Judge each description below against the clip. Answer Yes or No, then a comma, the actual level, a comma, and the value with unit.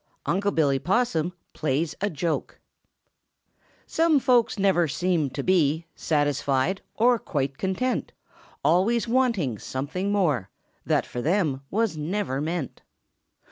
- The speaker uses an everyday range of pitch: No, wide, 5.9 semitones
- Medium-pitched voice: Yes, medium, 175 Hz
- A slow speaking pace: Yes, slow, 115 wpm